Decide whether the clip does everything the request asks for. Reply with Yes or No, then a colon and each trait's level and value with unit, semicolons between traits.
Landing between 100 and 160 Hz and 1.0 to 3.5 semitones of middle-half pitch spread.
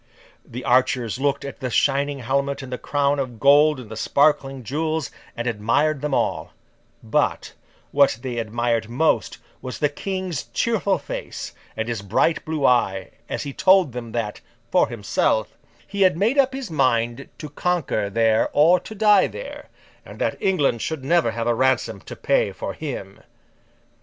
No: medium, 140 Hz; average, 5.1 semitones